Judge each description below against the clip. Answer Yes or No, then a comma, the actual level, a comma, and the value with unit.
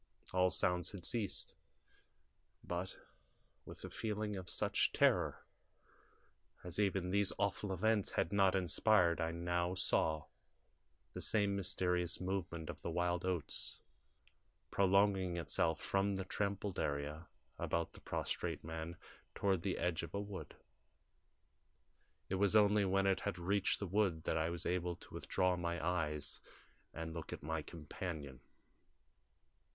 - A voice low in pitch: Yes, very low, 90 Hz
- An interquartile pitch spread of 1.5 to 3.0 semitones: Yes, average, 2.7 semitones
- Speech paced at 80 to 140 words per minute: Yes, slow, 135 wpm